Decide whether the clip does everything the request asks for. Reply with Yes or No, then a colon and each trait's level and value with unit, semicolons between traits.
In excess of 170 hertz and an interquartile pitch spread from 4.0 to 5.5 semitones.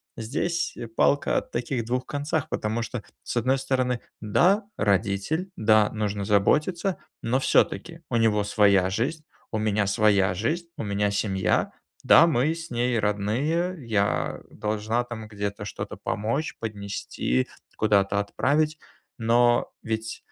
No: low, 115 Hz; average, 4.9 semitones